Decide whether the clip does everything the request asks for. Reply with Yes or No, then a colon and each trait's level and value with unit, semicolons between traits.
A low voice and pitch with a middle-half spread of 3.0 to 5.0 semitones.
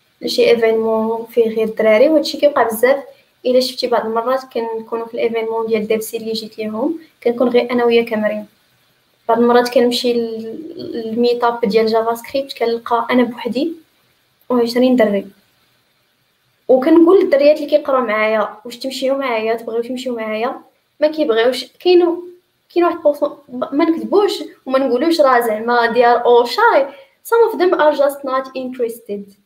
No: high, 245 Hz; average, 3.8 semitones